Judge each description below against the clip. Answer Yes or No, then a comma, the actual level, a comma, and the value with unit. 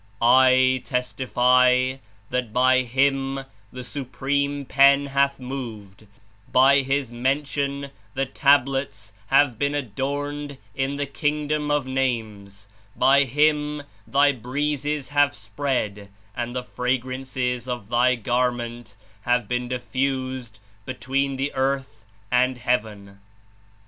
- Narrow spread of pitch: Yes, narrow, 2.2 semitones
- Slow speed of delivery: Yes, slow, 110 wpm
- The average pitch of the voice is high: No, low, 130 Hz